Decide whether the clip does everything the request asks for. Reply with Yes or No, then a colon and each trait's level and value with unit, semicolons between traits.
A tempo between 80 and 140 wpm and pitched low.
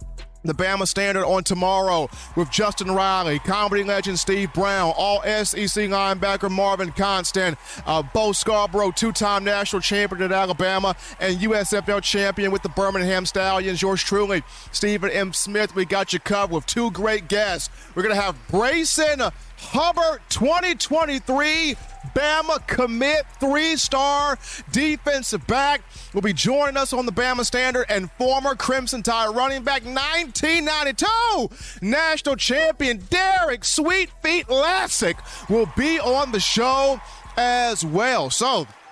No: slow, 135 wpm; high, 210 Hz